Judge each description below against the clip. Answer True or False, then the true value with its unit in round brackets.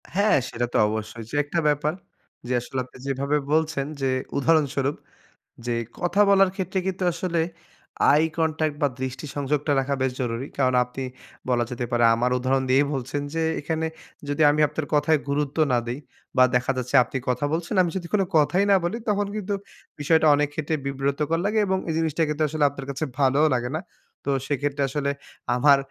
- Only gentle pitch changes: False (3.4 semitones)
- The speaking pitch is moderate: True (145 Hz)